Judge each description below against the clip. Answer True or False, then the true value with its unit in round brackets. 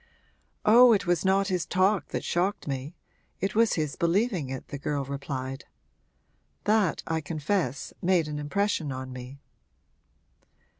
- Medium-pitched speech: True (165 Hz)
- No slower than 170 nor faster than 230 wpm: False (140 wpm)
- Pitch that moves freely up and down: True (5.9 semitones)